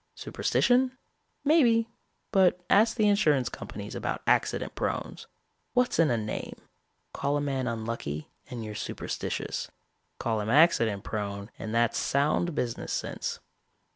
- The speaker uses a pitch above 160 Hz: No, medium, 140 Hz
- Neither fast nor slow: No, slow, 130 wpm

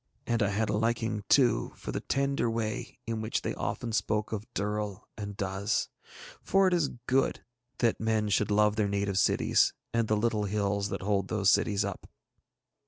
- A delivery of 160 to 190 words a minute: Yes, average, 180 wpm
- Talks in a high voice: No, low, 105 Hz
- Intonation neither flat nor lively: No, narrow, 2.1 semitones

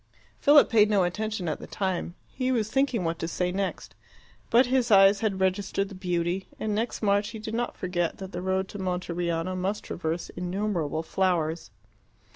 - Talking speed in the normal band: Yes, average, 180 wpm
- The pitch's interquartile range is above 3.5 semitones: No, average, 3.2 semitones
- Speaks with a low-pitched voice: No, high, 190 Hz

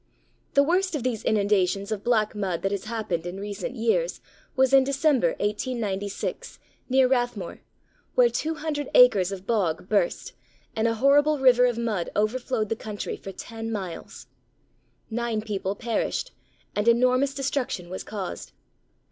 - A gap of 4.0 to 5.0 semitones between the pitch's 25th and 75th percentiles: Yes, average, 4.4 semitones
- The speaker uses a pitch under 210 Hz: No, high, 225 Hz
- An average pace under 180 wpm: Yes, average, 145 wpm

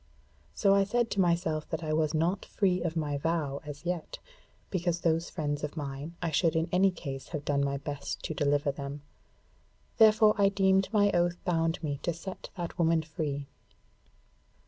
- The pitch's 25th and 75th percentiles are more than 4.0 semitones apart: No, average, 3.7 semitones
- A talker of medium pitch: Yes, medium, 165 Hz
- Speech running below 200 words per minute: Yes, average, 180 wpm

